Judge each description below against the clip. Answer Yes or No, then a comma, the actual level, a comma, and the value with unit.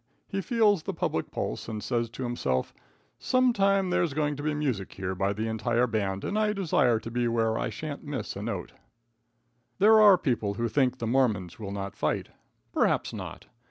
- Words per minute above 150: Yes, average, 190 wpm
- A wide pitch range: Yes, wide, 8.2 semitones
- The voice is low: Yes, low, 125 Hz